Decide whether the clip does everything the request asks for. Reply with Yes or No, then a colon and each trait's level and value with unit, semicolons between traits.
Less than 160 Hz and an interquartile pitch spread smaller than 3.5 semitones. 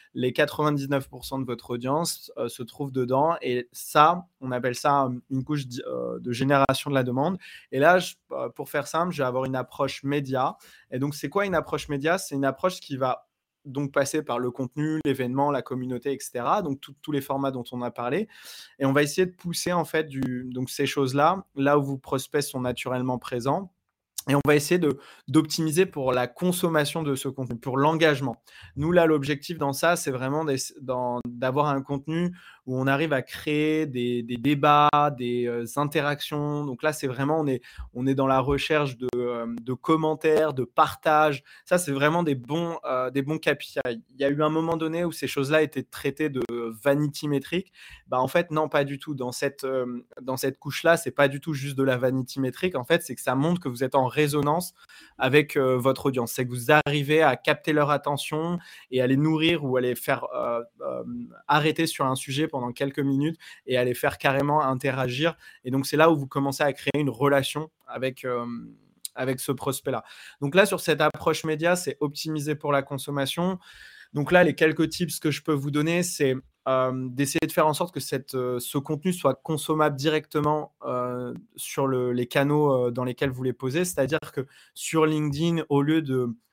Yes: medium, 140 Hz; average, 2.9 semitones